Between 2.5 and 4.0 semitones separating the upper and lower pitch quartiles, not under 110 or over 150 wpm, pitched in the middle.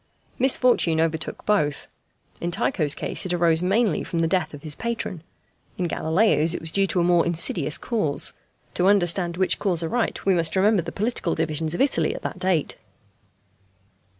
No: average, 3.5 semitones; average, 175 wpm; medium, 175 Hz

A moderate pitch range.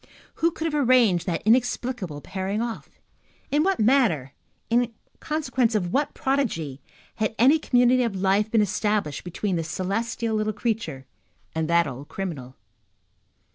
No: wide, 5.9 semitones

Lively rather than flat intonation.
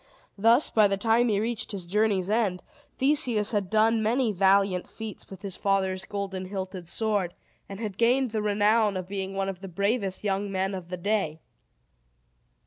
No: narrow, 2.4 semitones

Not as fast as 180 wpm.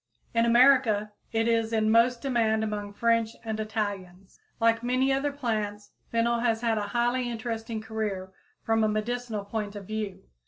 Yes: average, 160 wpm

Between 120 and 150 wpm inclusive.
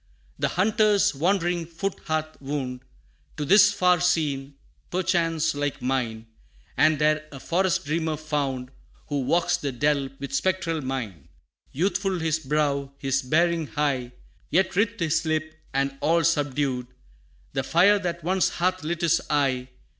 Yes: average, 140 wpm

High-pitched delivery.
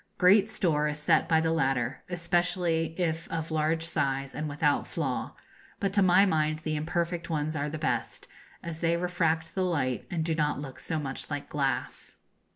No: medium, 160 Hz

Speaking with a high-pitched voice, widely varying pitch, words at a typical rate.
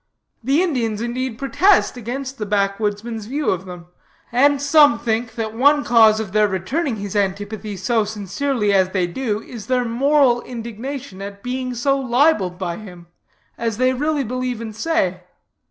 No: high, 230 Hz; average, 4.3 semitones; average, 165 wpm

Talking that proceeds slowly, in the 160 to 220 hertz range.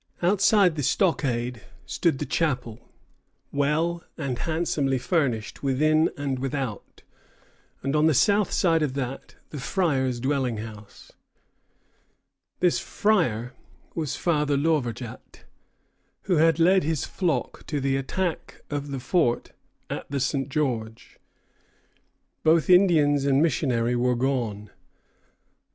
No: slow, 115 wpm; medium, 140 Hz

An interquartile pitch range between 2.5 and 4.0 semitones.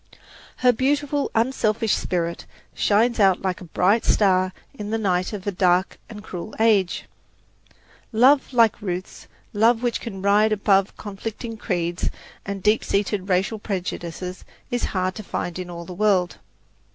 Yes: average, 3.4 semitones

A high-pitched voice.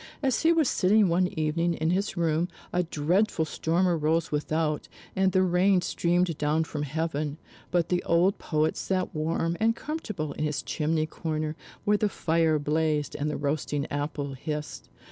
No: medium, 160 Hz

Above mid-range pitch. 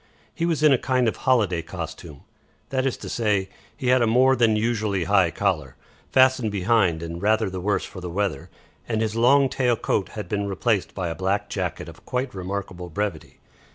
No: low, 105 Hz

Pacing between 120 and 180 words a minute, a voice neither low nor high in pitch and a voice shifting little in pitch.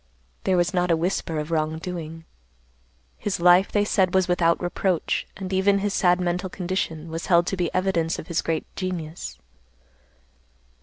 Yes: average, 165 wpm; medium, 175 Hz; narrow, 2.3 semitones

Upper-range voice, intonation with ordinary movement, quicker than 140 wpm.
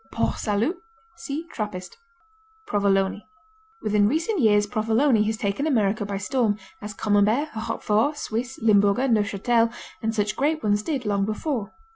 No: high, 220 Hz; average, 4.1 semitones; slow, 135 wpm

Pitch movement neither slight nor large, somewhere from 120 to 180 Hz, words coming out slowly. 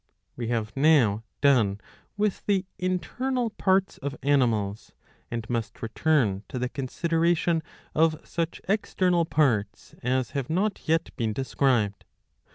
No: wide, 6.8 semitones; medium, 140 Hz; slow, 125 wpm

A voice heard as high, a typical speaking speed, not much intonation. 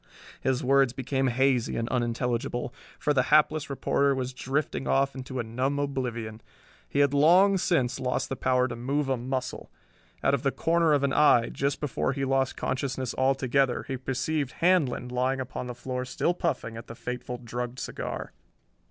No: low, 130 Hz; average, 175 wpm; narrow, 2.1 semitones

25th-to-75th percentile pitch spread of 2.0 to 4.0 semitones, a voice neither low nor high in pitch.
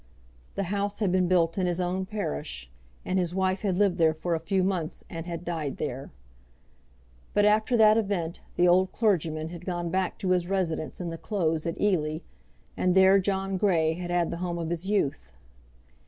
Yes: average, 2.7 semitones; medium, 180 Hz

